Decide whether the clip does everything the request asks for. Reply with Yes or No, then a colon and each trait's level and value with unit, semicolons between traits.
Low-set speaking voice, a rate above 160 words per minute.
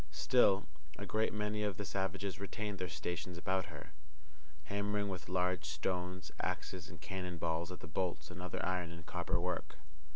Yes: very low, 90 Hz; average, 170 wpm